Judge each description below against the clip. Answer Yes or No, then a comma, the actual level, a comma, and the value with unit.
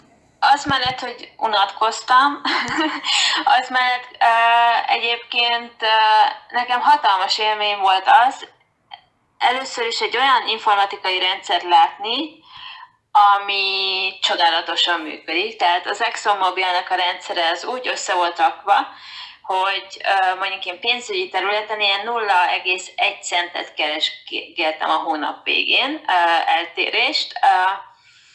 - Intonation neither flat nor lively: No, wide, 8.6 semitones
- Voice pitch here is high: Yes, high, 220 Hz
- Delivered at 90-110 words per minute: Yes, slow, 105 wpm